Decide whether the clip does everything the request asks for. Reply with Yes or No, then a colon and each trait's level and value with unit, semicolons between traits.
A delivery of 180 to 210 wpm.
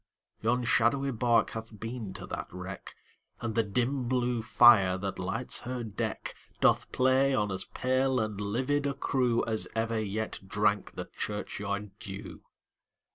No: slow, 135 wpm